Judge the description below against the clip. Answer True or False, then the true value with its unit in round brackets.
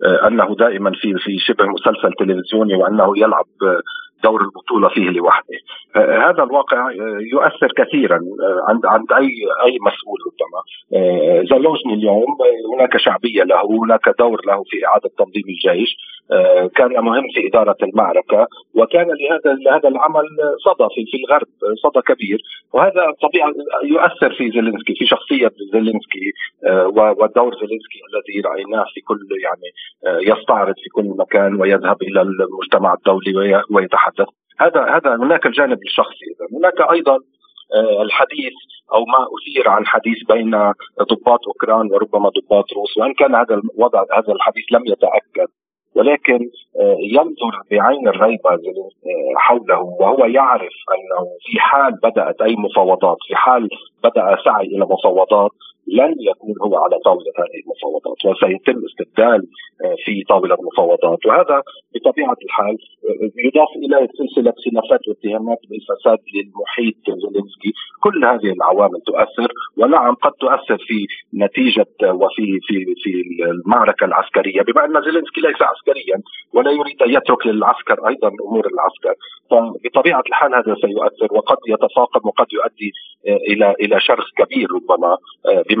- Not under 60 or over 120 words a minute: False (130 wpm)